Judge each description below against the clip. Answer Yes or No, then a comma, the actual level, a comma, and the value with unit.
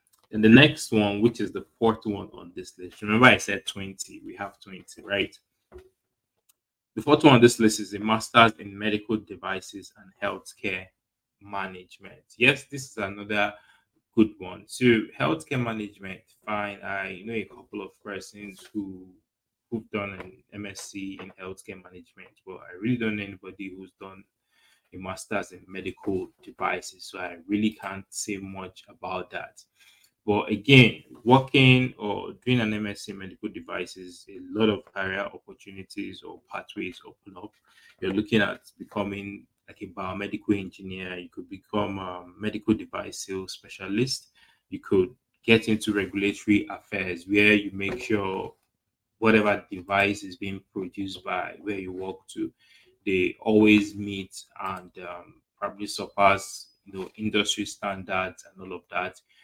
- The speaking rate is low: No, average, 155 wpm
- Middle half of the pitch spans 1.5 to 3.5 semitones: Yes, narrow, 2.4 semitones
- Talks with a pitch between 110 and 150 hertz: No, low, 100 Hz